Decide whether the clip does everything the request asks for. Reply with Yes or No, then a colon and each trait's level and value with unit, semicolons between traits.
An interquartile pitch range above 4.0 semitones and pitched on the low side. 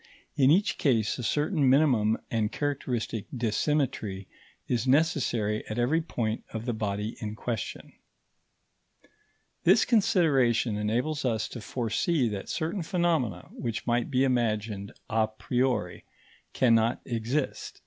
Yes: average, 4.8 semitones; low, 120 Hz